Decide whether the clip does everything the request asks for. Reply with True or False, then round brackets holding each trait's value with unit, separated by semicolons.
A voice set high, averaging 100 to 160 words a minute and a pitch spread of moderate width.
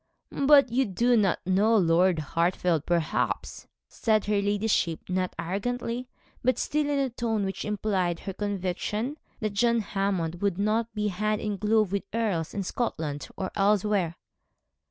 True (205 Hz; 150 wpm; 3.5 semitones)